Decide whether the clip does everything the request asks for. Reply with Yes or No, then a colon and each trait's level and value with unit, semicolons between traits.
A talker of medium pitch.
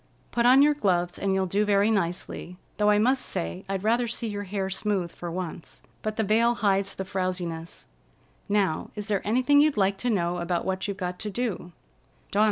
No: high, 200 Hz